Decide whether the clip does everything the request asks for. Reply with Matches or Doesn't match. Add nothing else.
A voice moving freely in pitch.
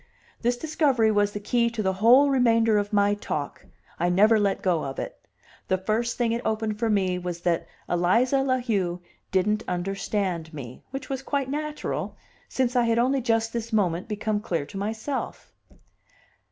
Doesn't match